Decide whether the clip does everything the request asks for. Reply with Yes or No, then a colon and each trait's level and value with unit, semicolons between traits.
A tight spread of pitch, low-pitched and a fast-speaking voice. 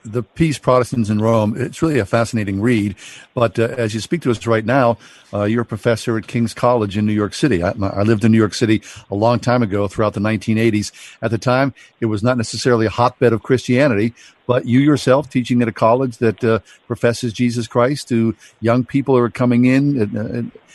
Yes: narrow, 2.1 semitones; low, 115 Hz; fast, 220 wpm